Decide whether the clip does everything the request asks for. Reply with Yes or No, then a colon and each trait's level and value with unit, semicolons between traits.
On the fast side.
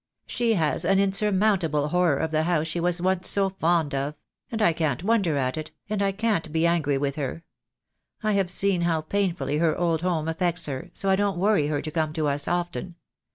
Yes: fast, 210 wpm